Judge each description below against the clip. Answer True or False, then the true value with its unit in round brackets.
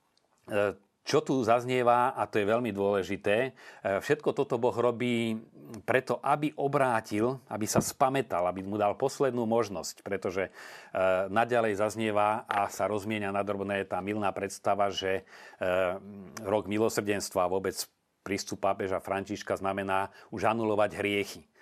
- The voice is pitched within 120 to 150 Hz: False (105 Hz)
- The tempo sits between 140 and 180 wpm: False (120 wpm)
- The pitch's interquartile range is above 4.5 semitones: False (2.8 semitones)